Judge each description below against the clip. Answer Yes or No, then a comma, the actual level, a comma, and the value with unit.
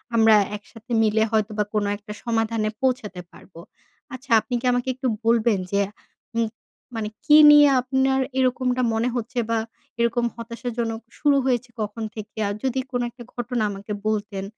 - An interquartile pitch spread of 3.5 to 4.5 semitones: No, average, 2.8 semitones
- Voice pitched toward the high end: Yes, high, 230 Hz